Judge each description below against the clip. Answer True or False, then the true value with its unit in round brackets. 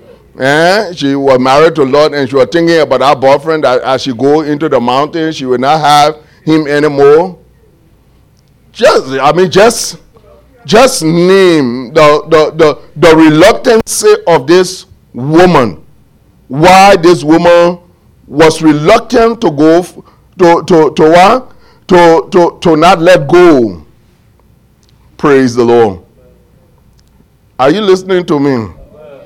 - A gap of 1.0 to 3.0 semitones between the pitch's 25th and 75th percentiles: False (4.1 semitones)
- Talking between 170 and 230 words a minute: False (135 wpm)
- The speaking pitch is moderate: True (160 Hz)